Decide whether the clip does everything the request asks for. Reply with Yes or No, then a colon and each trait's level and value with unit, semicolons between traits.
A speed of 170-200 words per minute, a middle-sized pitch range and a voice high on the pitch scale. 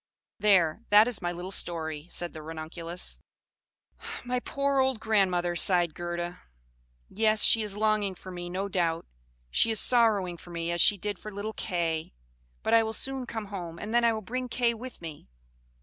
Yes: average, 180 wpm; average, 4.3 semitones; high, 195 Hz